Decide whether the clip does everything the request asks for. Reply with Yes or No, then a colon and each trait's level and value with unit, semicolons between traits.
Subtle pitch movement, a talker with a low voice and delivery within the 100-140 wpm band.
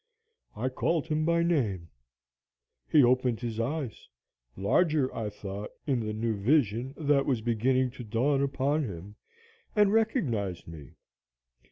No: wide, 5.5 semitones; low, 125 Hz; slow, 135 wpm